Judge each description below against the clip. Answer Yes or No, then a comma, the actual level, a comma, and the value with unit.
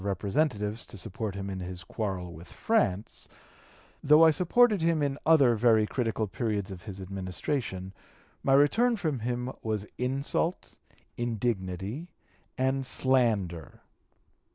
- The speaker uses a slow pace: Yes, slow, 130 wpm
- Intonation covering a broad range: Yes, wide, 6.2 semitones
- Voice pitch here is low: Yes, low, 115 Hz